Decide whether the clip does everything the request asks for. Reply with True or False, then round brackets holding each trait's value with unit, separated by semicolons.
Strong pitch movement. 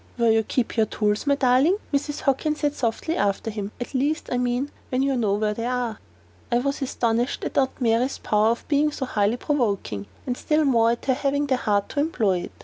False (3.9 semitones)